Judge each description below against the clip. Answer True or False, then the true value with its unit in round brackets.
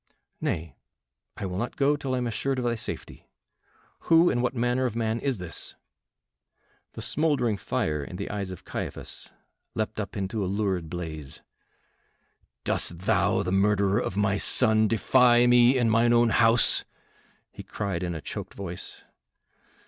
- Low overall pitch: True (110 Hz)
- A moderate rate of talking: True (160 wpm)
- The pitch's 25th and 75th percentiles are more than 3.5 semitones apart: True (4.3 semitones)